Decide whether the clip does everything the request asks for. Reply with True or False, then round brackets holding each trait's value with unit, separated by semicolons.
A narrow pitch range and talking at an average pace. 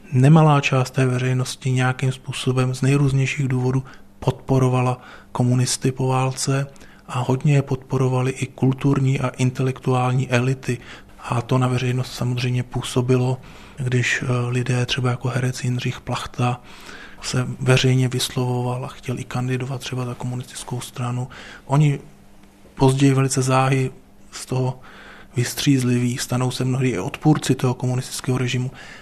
True (1.0 semitones; 125 wpm)